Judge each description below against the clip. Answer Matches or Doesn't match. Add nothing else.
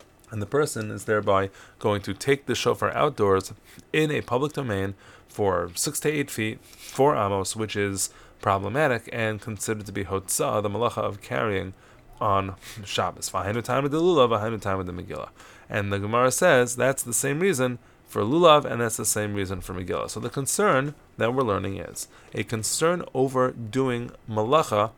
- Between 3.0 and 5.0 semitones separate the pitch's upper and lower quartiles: Matches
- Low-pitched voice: Matches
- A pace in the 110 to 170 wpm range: Doesn't match